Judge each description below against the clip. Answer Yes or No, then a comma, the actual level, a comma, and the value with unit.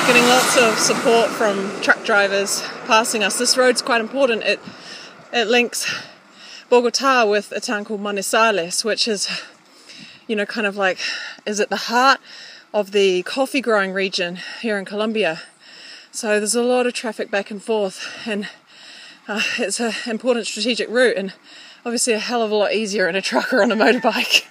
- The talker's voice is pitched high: Yes, high, 225 Hz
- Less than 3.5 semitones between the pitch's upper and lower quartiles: Yes, average, 3.1 semitones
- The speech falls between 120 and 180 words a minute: Yes, average, 175 wpm